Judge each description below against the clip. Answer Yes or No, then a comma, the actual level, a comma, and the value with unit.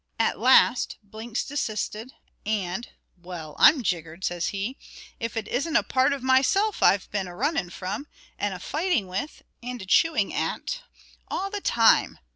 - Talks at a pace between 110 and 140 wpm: No, average, 160 wpm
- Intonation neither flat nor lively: No, wide, 6.3 semitones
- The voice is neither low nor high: No, high, 225 Hz